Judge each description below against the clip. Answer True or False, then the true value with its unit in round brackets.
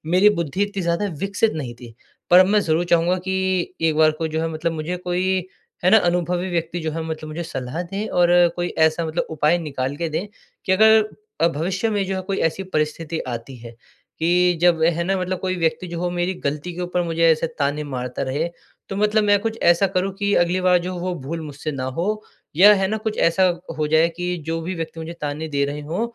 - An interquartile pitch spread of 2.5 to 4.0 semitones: True (3.0 semitones)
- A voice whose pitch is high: False (170 Hz)